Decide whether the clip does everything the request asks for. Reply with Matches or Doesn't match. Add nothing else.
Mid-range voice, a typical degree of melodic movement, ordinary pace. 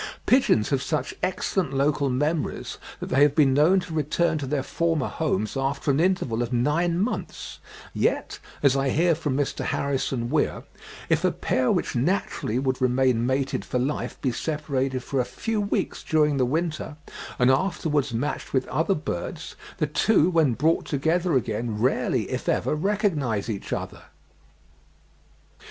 Matches